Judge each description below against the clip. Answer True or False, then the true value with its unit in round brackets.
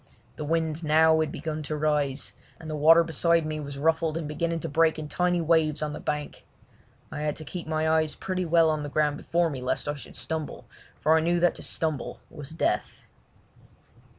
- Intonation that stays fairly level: True (1.6 semitones)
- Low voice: False (155 Hz)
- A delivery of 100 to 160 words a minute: False (205 wpm)